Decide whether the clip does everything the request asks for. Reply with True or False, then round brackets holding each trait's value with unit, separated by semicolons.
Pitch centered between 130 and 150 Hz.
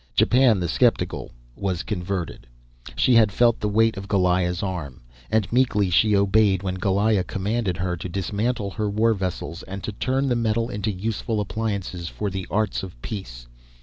False (100 Hz)